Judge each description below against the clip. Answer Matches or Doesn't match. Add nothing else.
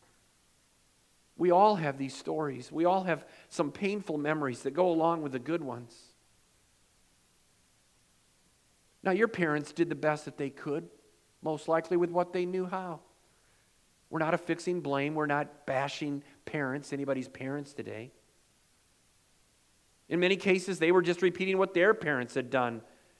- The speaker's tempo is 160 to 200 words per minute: Doesn't match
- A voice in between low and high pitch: Matches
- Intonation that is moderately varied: Matches